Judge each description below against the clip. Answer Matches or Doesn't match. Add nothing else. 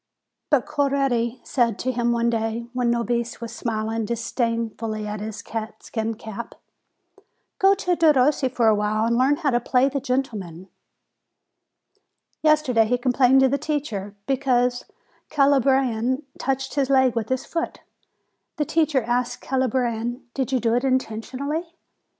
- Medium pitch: Doesn't match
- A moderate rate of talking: Matches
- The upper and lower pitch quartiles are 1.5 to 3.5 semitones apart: Matches